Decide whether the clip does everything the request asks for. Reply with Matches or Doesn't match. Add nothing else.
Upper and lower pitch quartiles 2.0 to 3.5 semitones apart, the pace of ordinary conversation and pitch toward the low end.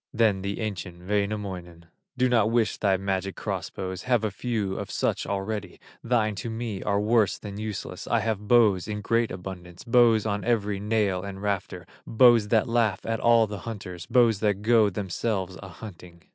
Matches